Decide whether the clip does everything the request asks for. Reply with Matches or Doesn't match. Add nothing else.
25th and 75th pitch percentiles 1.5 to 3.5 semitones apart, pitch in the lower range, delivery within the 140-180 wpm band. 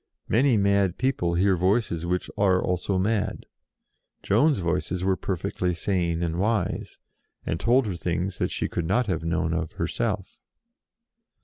Matches